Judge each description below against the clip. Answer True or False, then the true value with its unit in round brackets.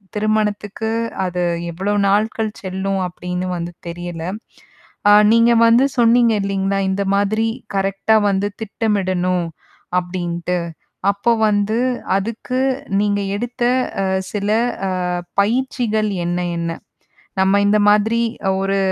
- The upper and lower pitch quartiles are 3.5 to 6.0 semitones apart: False (2.7 semitones)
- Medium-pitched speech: False (200 Hz)